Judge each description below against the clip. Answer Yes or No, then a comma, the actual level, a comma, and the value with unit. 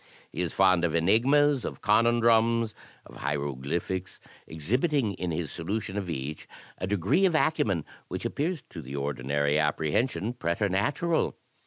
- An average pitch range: No, wide, 7.0 semitones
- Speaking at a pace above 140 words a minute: No, slow, 135 wpm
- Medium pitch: No, very low, 95 Hz